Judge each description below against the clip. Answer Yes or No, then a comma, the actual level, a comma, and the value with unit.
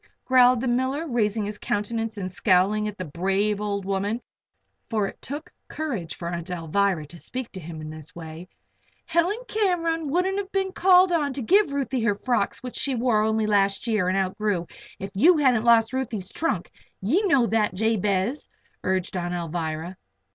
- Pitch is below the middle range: No, high, 215 Hz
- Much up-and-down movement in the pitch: Yes, wide, 5.9 semitones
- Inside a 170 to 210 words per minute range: Yes, average, 175 wpm